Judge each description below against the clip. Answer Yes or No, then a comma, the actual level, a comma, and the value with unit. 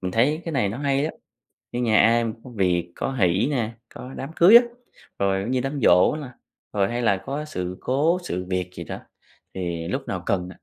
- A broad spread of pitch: Yes, wide, 6.9 semitones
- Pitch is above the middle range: No, low, 115 Hz